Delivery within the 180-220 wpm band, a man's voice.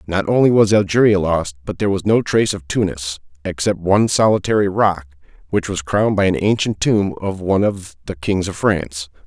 Yes: average, 195 wpm; male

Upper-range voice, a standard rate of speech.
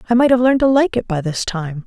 No: high, 220 Hz; fast, 320 wpm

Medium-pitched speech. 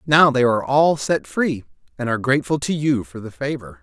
No: low, 130 Hz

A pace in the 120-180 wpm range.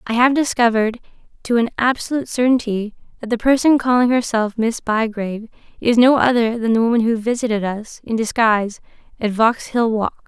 Yes: average, 165 wpm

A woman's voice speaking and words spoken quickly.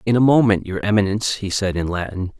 No: male; fast, 225 wpm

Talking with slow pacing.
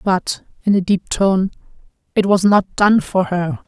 No: average, 180 wpm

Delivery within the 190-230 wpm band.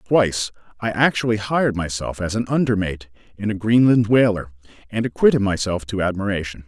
No: average, 160 wpm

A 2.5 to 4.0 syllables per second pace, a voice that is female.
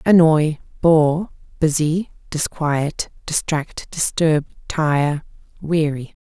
Yes: 3.0 syllables/s; female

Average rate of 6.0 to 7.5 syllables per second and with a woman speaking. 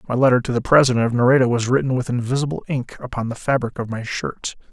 No: 6.7 syllables/s; male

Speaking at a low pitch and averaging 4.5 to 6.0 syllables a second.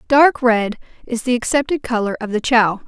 No: high, 240 Hz; 5.0 syllables/s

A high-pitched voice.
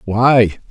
No: low, 115 Hz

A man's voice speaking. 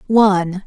No: female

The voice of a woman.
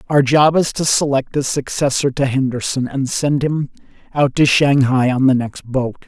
No: male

